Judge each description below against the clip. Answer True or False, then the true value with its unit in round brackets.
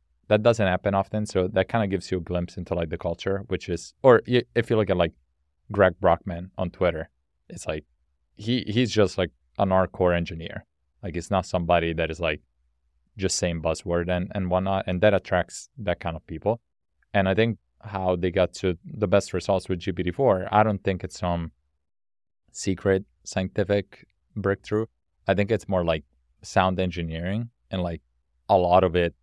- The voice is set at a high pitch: False (90 Hz)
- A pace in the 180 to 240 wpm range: True (185 wpm)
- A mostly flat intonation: False (3.0 semitones)